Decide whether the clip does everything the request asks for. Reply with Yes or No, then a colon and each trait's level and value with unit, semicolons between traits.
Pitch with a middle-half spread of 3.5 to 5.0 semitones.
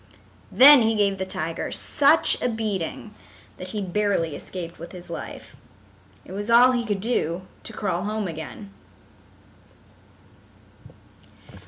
Yes: average, 3.9 semitones